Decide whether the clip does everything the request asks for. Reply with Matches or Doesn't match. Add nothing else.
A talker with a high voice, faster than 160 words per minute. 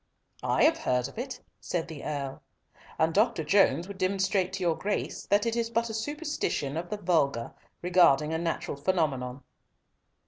Doesn't match